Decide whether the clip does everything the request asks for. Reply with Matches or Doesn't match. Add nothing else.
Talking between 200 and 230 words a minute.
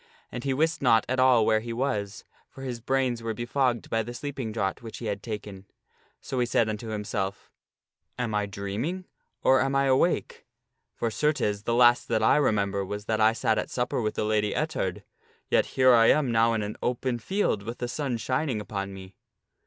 Matches